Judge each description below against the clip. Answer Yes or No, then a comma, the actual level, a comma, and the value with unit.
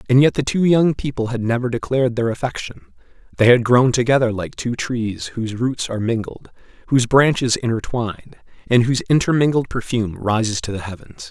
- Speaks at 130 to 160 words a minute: No, average, 175 wpm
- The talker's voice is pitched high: No, low, 120 Hz